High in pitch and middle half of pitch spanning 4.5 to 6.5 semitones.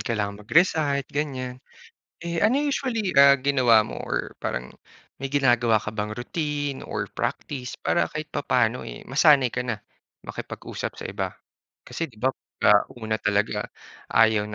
No: low, 130 Hz; average, 4.9 semitones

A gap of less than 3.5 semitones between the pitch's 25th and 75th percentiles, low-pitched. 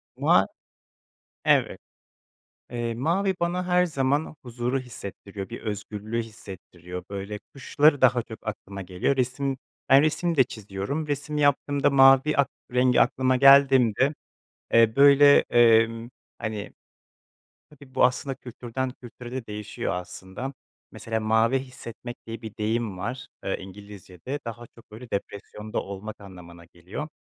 No: average, 4.4 semitones; low, 120 Hz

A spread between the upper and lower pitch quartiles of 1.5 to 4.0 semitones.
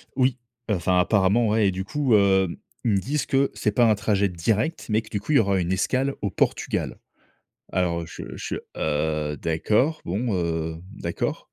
No: average, 4.6 semitones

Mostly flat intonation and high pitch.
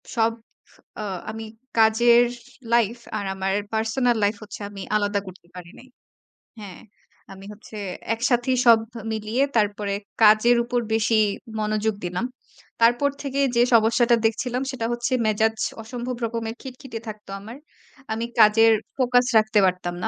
Yes: narrow, 2.2 semitones; high, 225 Hz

